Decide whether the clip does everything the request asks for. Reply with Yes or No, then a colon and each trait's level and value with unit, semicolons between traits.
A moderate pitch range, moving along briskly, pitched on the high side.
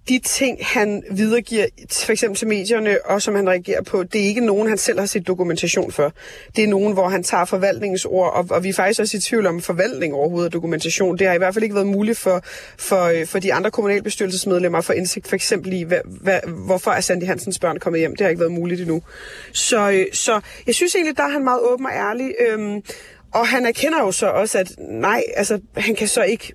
Yes: average, 3.3 semitones; fast, 230 wpm; high, 200 Hz